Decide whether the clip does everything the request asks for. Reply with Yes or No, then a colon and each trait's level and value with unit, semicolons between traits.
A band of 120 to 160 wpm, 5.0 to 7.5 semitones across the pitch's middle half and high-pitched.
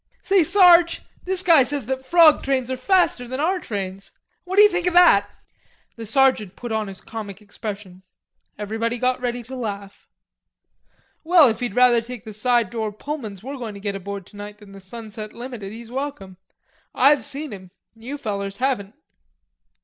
No: average, 170 wpm; average, 5.3 semitones; high, 235 Hz